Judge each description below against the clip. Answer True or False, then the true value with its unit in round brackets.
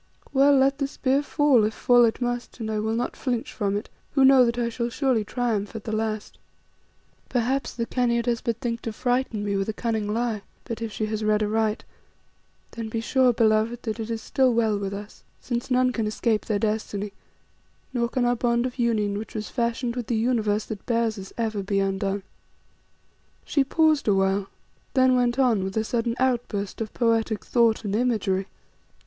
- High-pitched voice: True (230 Hz)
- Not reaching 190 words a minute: False (195 wpm)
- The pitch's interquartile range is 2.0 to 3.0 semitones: True (2.4 semitones)